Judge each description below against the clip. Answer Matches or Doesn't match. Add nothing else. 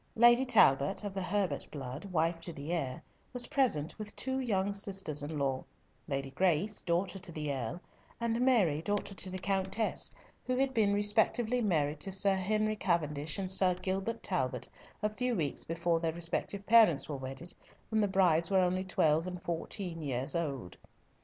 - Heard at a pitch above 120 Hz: Matches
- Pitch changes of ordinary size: Matches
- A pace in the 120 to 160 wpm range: Doesn't match